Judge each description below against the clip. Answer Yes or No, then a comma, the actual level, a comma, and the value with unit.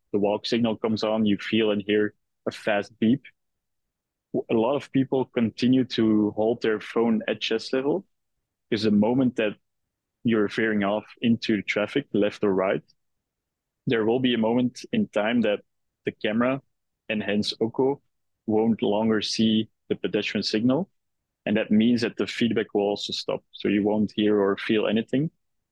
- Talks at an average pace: Yes, average, 165 wpm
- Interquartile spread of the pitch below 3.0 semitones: Yes, narrow, 2.5 semitones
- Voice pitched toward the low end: Yes, low, 110 Hz